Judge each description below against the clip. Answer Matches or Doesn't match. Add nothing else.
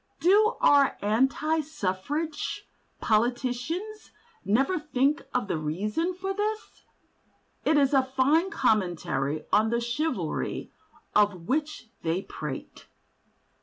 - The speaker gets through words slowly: Matches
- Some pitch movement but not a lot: Doesn't match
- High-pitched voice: Matches